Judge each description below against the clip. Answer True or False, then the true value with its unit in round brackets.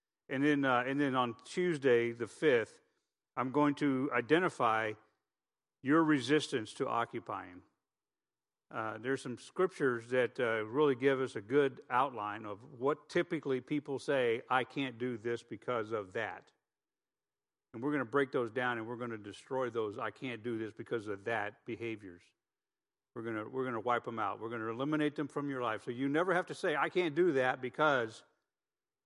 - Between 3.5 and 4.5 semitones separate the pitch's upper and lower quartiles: True (4.0 semitones)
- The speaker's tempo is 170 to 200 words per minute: True (185 wpm)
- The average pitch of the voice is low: True (130 Hz)